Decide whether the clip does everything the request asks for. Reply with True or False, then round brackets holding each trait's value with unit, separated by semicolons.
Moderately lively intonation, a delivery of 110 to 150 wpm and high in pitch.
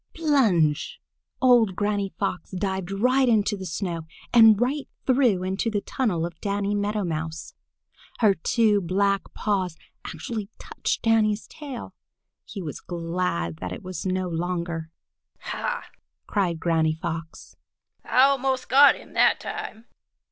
True (4.9 semitones; 135 wpm; 200 Hz)